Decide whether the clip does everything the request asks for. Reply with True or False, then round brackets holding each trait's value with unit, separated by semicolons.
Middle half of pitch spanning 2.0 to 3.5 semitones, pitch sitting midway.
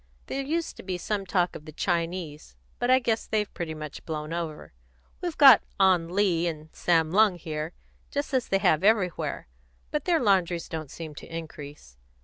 False (5.1 semitones; 175 Hz)